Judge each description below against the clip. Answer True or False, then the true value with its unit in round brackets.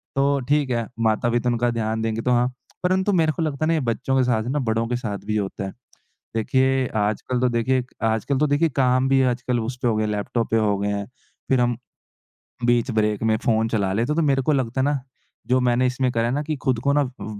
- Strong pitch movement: False (3.1 semitones)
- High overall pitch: False (125 Hz)